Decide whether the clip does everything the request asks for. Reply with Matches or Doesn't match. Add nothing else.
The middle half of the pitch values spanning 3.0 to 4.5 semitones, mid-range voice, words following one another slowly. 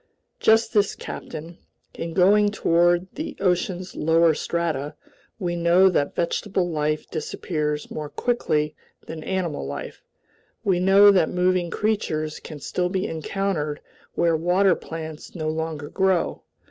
Matches